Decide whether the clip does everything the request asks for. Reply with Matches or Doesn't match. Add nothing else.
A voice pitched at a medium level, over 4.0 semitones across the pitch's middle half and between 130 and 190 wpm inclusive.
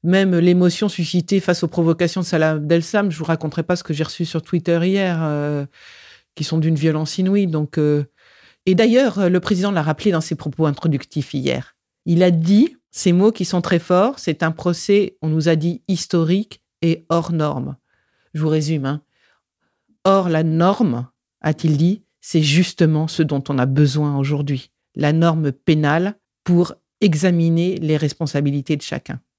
Doesn't match